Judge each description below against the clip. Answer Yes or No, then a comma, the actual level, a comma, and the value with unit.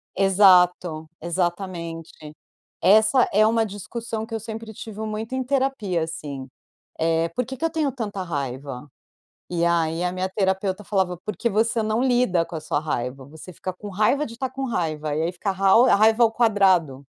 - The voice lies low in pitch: No, high, 190 Hz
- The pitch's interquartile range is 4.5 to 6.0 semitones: Yes, average, 5.0 semitones